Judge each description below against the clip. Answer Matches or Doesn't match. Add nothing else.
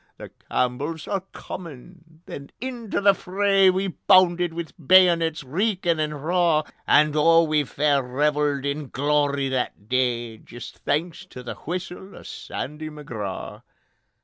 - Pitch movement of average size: Matches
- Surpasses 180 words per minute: Doesn't match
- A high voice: Doesn't match